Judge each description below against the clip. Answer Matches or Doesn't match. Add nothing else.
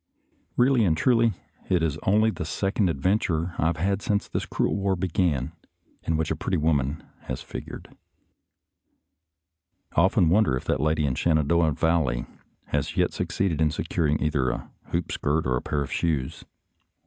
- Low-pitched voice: Matches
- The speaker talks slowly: Doesn't match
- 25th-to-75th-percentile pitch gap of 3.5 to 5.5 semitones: Matches